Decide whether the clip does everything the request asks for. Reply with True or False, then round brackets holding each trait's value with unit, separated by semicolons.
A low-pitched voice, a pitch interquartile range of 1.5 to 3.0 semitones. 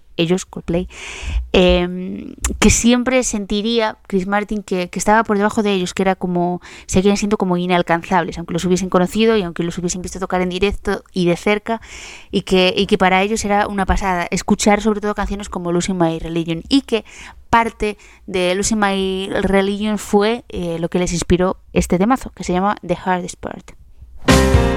False (190 Hz; 2.7 semitones)